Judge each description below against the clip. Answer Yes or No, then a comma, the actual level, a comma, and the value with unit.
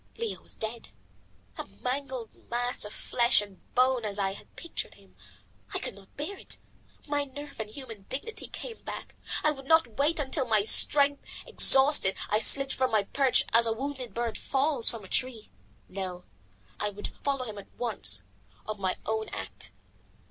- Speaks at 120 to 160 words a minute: No, average, 175 wpm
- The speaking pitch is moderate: No, high, 240 Hz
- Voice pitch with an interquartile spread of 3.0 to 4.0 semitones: No, average, 5.0 semitones